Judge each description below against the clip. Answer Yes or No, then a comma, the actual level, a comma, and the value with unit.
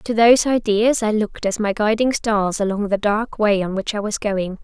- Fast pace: Yes, fast, 235 wpm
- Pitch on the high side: Yes, high, 210 Hz